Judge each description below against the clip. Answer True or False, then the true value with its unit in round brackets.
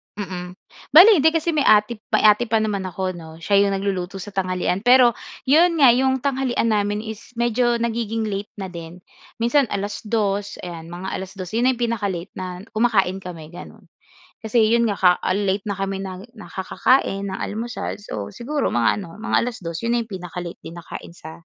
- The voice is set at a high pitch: True (205 Hz)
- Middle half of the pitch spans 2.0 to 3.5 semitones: False (4.2 semitones)